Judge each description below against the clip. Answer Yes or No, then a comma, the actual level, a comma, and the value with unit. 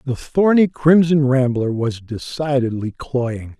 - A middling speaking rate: No, slow, 115 wpm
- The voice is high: No, low, 135 Hz